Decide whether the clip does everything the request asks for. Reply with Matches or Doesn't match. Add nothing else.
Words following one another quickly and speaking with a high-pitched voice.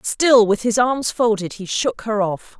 Matches